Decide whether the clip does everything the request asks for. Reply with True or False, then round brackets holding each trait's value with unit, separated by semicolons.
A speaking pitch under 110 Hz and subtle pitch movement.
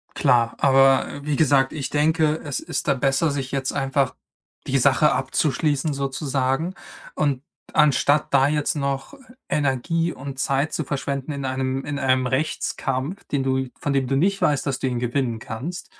False (140 Hz; 2.0 semitones)